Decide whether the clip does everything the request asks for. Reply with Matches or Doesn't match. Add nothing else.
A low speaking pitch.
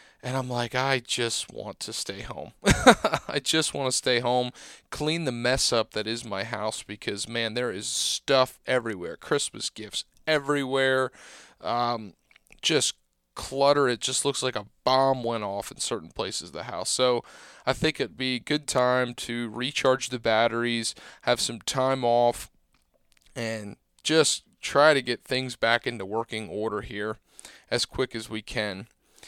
Matches